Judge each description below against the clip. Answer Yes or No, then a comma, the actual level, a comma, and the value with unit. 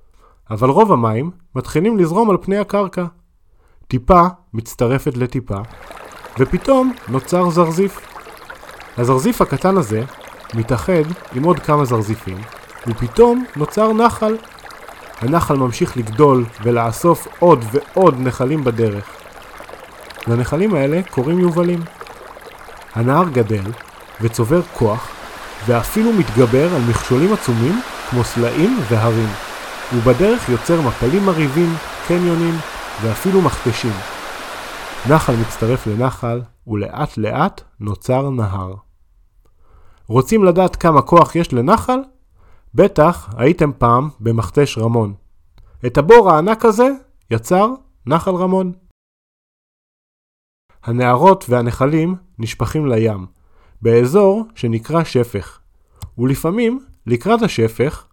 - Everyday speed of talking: No, slow, 95 wpm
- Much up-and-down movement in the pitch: Yes, wide, 7.6 semitones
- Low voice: Yes, low, 130 Hz